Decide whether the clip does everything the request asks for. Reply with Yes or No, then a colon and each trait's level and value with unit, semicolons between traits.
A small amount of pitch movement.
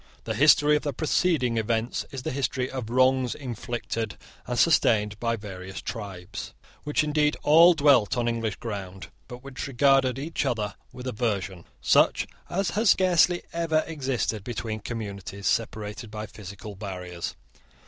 No: average, 5.1 semitones